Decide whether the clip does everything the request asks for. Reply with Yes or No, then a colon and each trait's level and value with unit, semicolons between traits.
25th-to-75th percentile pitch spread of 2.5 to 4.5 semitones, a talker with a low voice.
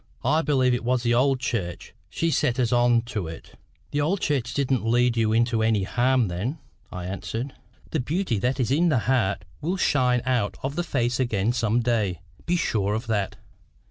Yes: average, 3.2 semitones; low, 120 Hz